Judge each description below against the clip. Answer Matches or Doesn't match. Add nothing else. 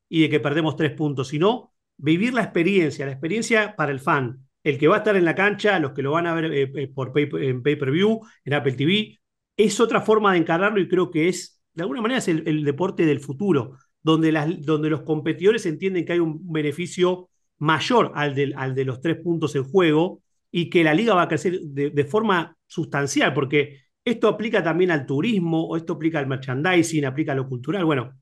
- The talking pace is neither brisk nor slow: Doesn't match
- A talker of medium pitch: Matches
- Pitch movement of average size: Matches